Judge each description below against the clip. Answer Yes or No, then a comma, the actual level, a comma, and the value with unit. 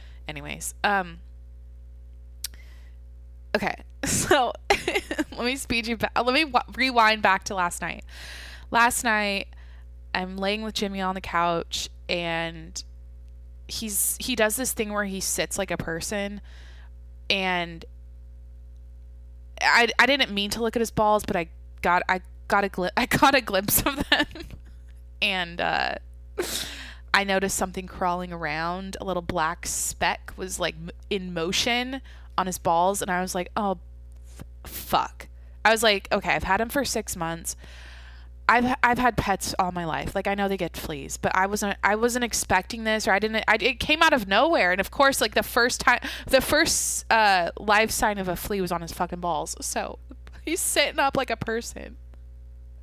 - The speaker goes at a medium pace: Yes, average, 175 wpm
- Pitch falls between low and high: Yes, medium, 180 Hz